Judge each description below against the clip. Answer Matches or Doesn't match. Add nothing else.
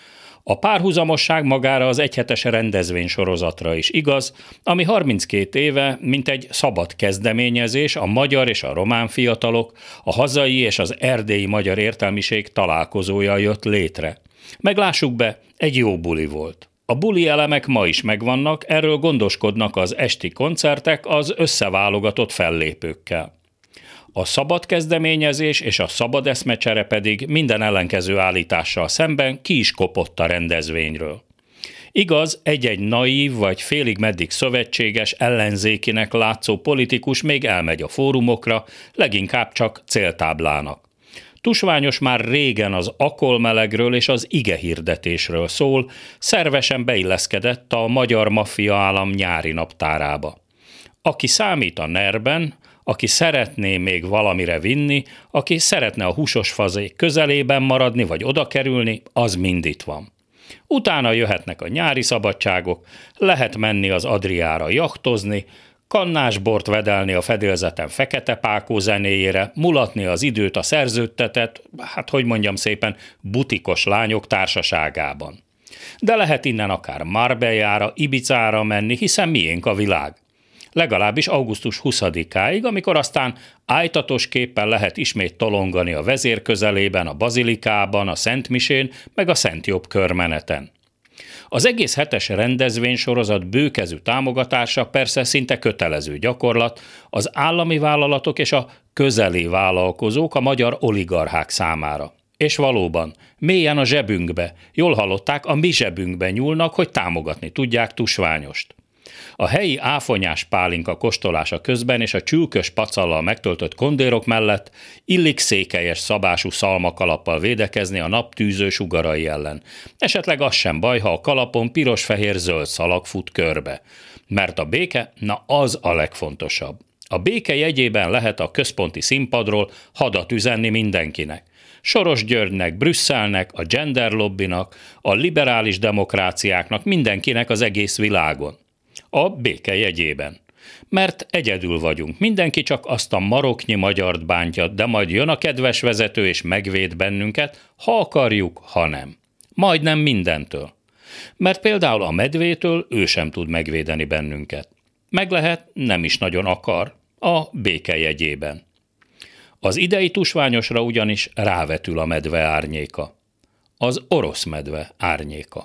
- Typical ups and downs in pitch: Doesn't match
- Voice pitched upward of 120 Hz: Doesn't match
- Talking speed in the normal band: Matches